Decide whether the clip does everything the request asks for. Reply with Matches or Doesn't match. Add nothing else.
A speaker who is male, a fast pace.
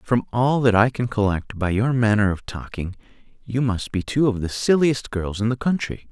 Matches